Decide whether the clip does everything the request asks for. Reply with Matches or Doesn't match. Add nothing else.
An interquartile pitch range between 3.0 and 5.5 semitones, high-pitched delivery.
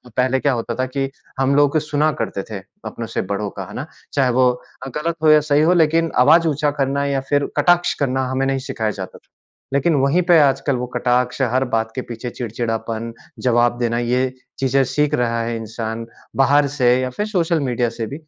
Doesn't match